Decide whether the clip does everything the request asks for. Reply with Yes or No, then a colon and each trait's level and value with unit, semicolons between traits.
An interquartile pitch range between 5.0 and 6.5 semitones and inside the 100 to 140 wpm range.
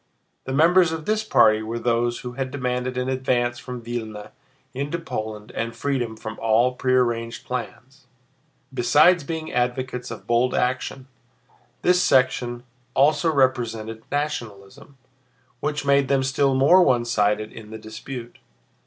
No: average, 3.1 semitones; slow, 135 wpm